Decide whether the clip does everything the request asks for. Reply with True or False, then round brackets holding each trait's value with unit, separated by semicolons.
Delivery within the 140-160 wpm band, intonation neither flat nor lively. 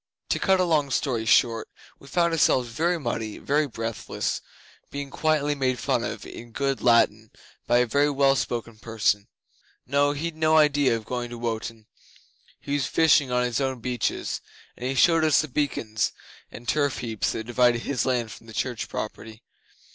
False (175 wpm; 3.8 semitones)